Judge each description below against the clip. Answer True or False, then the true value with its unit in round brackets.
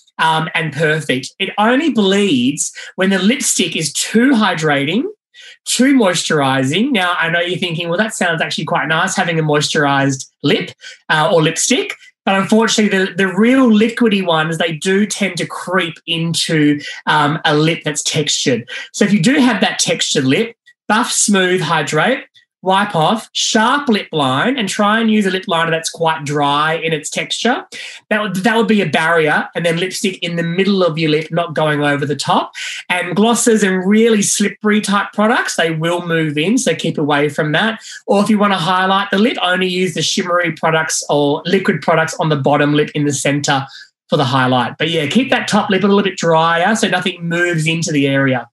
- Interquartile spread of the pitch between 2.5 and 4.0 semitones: False (5.1 semitones)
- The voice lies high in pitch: False (180 Hz)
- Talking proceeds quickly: False (195 wpm)